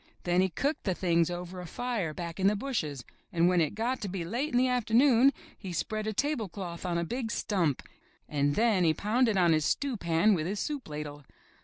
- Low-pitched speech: No, high, 190 Hz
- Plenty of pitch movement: Yes, wide, 5.7 semitones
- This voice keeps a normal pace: No, fast, 215 wpm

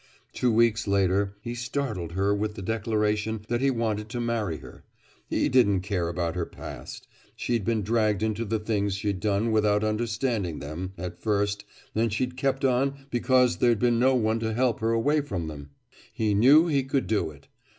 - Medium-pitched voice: No, low, 110 Hz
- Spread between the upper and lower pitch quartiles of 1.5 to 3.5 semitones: Yes, average, 3.1 semitones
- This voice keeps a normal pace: Yes, average, 185 wpm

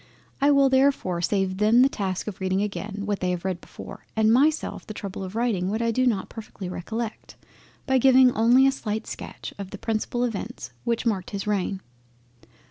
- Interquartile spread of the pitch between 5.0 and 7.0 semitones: No, average, 4.2 semitones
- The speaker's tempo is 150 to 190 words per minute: No, average, 200 wpm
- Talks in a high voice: Yes, high, 215 Hz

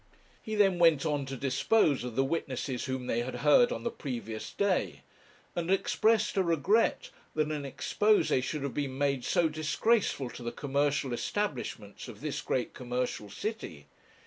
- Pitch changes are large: Yes, wide, 5.9 semitones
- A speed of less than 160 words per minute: No, average, 165 wpm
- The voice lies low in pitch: No, medium, 145 Hz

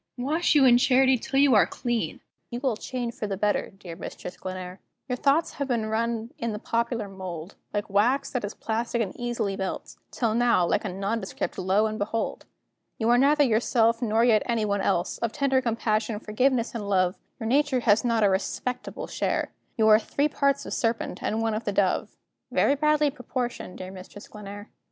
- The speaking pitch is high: Yes, high, 225 Hz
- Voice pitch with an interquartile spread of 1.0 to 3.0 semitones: No, average, 3.5 semitones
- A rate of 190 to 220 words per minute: Yes, average, 195 wpm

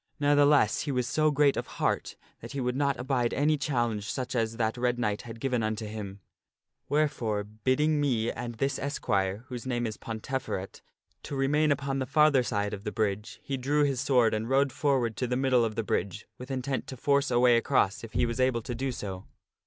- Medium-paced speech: No, fast, 215 wpm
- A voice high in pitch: No, low, 125 Hz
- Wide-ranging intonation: No, average, 3.8 semitones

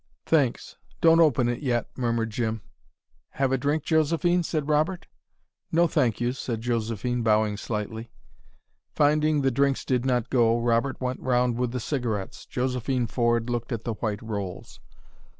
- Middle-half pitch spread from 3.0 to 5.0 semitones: Yes, average, 3.4 semitones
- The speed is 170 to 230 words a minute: No, average, 150 wpm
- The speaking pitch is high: No, low, 125 Hz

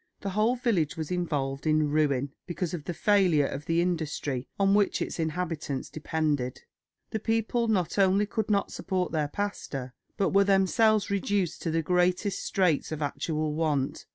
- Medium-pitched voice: Yes, medium, 175 Hz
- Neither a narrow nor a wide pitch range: Yes, average, 4.7 semitones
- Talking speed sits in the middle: Yes, average, 165 wpm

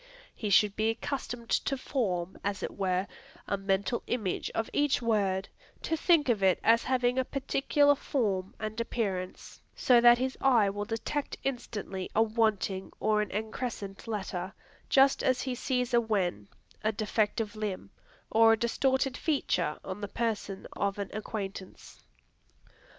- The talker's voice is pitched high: Yes, high, 220 Hz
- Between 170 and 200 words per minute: No, average, 150 wpm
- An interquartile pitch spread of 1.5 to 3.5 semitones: No, average, 3.9 semitones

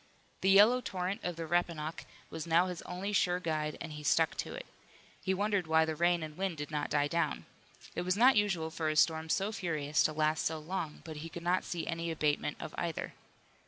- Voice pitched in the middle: Yes, medium, 165 Hz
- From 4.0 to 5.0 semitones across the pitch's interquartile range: No, average, 2.8 semitones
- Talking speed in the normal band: No, fast, 220 wpm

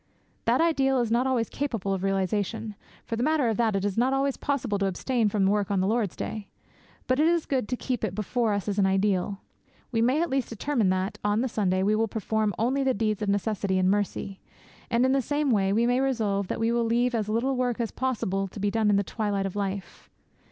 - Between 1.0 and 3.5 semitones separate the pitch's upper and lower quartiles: No, average, 3.9 semitones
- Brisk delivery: Yes, fast, 235 wpm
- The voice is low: No, high, 220 Hz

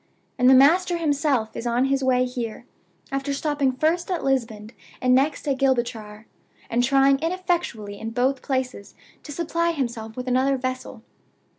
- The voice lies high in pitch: Yes, very high, 260 Hz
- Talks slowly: No, average, 155 wpm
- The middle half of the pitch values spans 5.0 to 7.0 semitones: No, average, 3.1 semitones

